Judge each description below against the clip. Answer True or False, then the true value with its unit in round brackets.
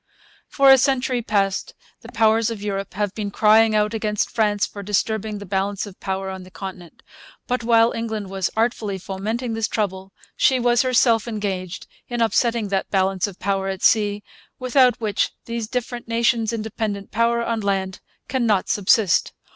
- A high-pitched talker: True (215 Hz)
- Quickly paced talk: False (165 wpm)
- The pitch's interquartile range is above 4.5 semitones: False (2.9 semitones)